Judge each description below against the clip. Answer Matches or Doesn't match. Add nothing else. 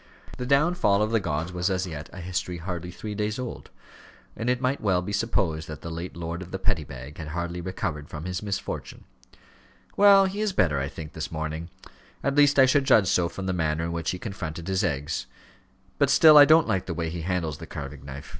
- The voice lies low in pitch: Matches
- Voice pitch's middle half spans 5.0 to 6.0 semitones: Matches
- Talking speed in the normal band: Doesn't match